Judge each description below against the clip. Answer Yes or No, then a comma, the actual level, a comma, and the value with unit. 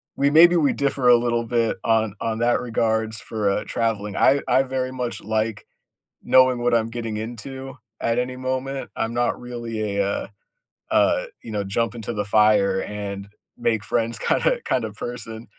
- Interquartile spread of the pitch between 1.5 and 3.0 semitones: Yes, narrow, 2.6 semitones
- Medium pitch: No, low, 115 Hz